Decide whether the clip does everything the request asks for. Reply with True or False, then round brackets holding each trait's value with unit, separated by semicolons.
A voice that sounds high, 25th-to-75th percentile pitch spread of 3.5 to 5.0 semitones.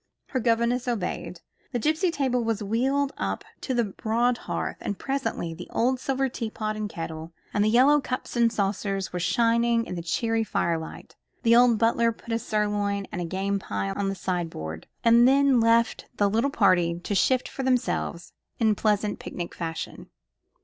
True (225 Hz; 3.9 semitones)